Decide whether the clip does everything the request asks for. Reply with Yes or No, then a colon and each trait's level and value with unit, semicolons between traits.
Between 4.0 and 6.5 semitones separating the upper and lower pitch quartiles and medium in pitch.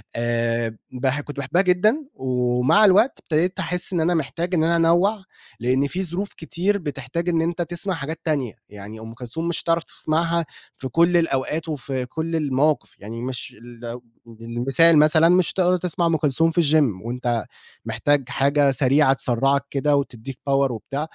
Yes: average, 4.9 semitones; medium, 150 Hz